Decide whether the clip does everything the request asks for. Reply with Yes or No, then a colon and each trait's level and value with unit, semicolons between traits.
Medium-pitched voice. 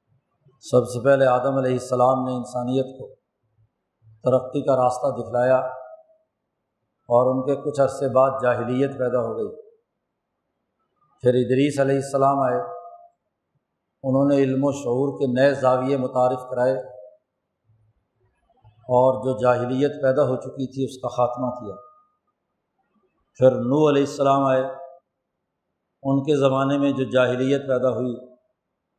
No: low, 130 Hz